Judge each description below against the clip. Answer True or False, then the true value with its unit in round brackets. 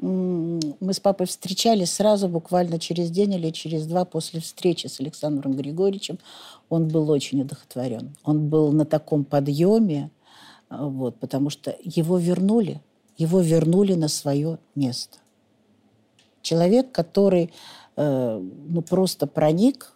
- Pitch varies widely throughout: False (3.8 semitones)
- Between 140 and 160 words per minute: False (120 wpm)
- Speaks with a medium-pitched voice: True (165 Hz)